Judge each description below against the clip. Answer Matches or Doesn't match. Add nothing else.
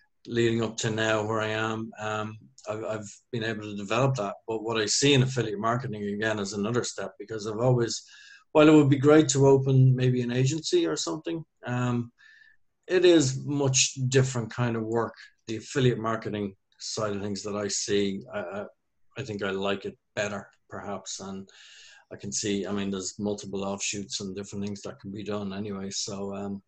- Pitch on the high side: Doesn't match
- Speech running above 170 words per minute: Matches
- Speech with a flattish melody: Doesn't match